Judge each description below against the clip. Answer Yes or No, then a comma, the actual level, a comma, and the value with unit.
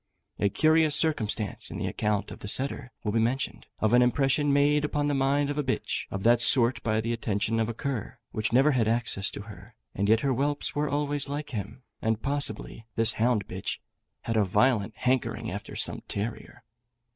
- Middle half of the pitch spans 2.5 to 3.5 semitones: No, average, 4.6 semitones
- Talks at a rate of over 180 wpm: Yes, average, 200 wpm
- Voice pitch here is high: No, low, 120 Hz